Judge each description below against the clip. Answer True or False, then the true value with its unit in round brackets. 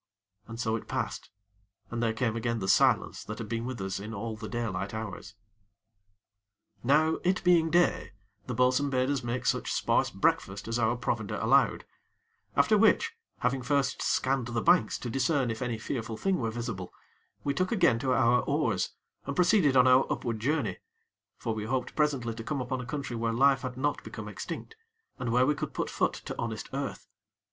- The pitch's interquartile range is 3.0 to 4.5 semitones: True (3.4 semitones)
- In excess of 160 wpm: True (190 wpm)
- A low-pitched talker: True (125 Hz)